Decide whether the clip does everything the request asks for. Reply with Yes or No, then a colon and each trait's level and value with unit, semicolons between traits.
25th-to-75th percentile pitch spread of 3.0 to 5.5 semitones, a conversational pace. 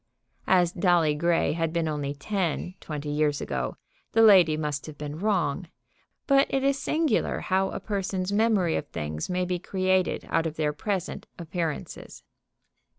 Yes: average, 4.1 semitones; average, 155 wpm